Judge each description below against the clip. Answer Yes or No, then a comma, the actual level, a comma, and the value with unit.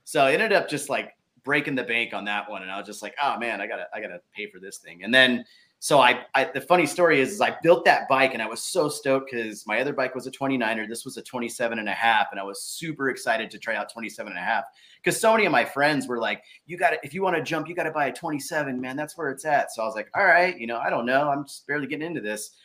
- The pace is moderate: No, fast, 315 wpm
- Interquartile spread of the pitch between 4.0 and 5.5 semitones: Yes, average, 4.7 semitones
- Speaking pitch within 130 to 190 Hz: Yes, low, 135 Hz